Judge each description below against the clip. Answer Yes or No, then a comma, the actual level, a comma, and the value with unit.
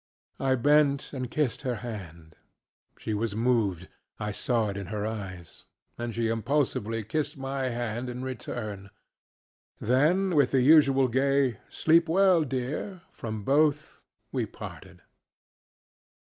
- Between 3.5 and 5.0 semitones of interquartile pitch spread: Yes, average, 4.5 semitones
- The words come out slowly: Yes, slow, 125 wpm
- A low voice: Yes, low, 125 Hz